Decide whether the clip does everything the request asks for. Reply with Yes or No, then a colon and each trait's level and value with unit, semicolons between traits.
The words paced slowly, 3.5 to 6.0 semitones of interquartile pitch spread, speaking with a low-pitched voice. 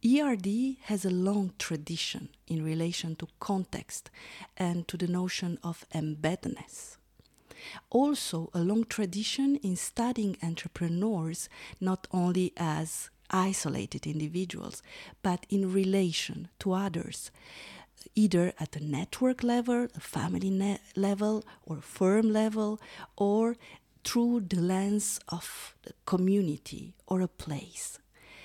No: slow, 110 wpm; average, 3.8 semitones; medium, 185 Hz